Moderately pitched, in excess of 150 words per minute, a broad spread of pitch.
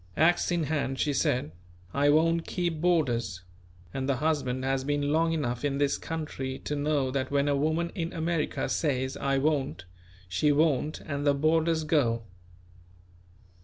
No: medium, 145 Hz; average, 160 wpm; average, 3.1 semitones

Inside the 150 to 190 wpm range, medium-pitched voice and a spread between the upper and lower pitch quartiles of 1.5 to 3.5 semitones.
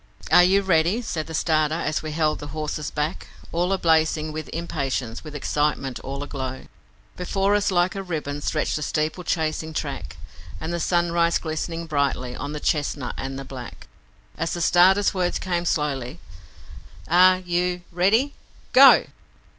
Yes: average, 155 wpm; medium, 160 Hz; average, 3.1 semitones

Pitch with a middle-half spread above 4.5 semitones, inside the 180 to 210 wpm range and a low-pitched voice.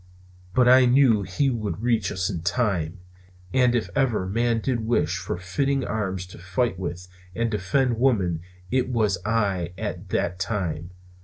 No: average, 5.1 semitones; average, 160 wpm; low, 105 Hz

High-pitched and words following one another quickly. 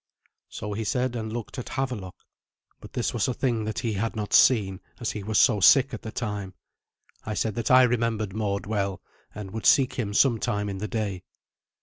No: low, 110 Hz; fast, 210 wpm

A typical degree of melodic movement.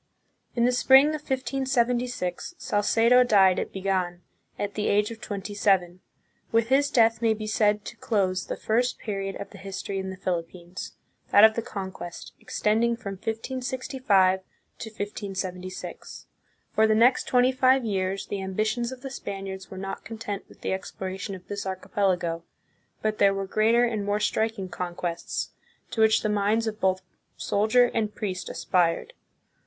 Yes: average, 3.3 semitones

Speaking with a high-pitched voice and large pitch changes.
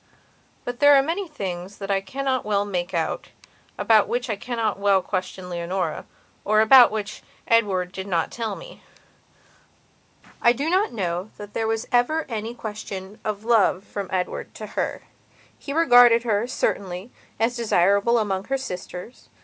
No: high, 215 Hz; average, 4.1 semitones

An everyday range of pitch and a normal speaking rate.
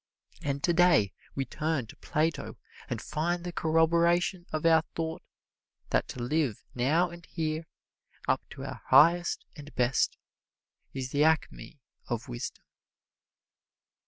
No: average, 3.6 semitones; slow, 130 wpm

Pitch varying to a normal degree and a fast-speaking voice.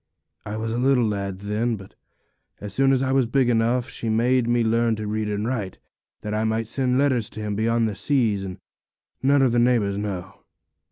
Yes: average, 3.0 semitones; fast, 210 wpm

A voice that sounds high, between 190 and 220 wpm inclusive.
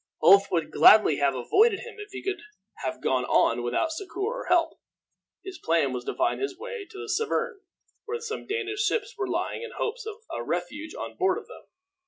Yes: very high, 395 Hz; fast, 205 wpm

